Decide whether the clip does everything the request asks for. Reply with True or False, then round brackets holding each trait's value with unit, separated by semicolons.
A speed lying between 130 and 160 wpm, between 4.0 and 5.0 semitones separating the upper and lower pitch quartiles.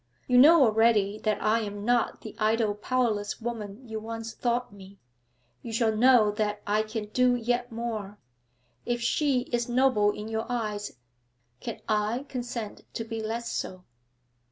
False (155 wpm; 2.4 semitones)